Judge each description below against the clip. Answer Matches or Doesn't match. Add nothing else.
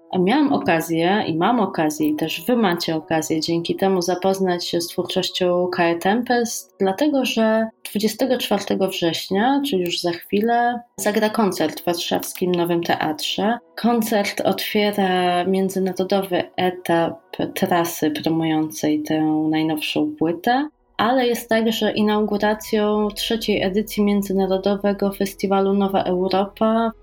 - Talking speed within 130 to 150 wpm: Doesn't match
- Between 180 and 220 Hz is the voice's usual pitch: Matches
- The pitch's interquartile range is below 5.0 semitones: Matches